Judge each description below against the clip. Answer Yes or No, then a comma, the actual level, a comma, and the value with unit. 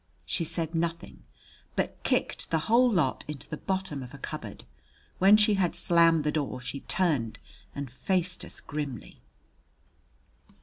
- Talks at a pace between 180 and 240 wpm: No, average, 145 wpm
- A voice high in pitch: No, medium, 165 Hz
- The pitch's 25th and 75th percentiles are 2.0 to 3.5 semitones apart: No, average, 4.5 semitones